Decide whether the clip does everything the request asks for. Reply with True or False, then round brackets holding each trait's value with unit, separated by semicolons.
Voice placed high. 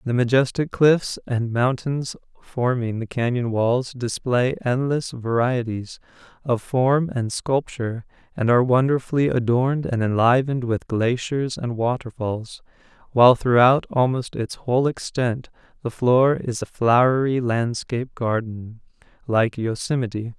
False (125 Hz)